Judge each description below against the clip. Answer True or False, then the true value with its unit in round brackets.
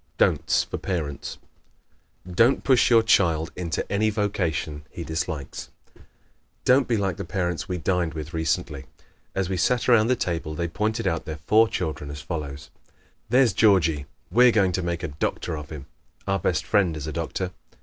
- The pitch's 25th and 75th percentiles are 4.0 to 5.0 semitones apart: True (4.7 semitones)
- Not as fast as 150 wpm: False (175 wpm)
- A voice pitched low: True (90 Hz)